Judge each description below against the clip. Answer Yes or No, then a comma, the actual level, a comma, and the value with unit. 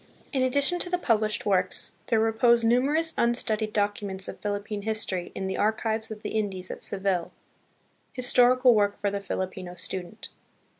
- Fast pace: No, average, 170 wpm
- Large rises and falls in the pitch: No, average, 3.3 semitones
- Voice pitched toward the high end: Yes, high, 215 Hz